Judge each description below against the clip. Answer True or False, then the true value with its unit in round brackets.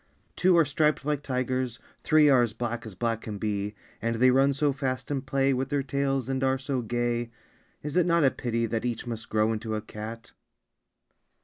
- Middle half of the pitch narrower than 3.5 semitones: True (3.1 semitones)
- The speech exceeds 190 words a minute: True (205 wpm)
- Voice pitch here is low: True (130 Hz)